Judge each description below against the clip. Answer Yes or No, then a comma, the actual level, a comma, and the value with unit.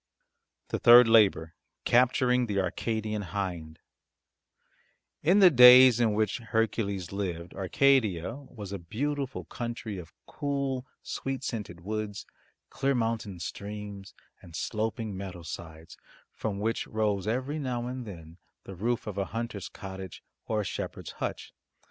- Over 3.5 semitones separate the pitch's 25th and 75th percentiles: Yes, average, 4.2 semitones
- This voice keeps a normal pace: No, slow, 130 wpm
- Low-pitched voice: Yes, low, 110 Hz